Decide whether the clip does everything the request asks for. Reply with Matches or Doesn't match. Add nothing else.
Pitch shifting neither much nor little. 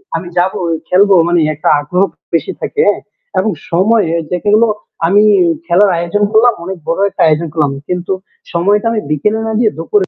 Matches